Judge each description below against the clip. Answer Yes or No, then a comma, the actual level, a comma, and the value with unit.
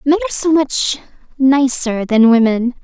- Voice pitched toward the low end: No, very high, 270 Hz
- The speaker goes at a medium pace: Yes, average, 150 wpm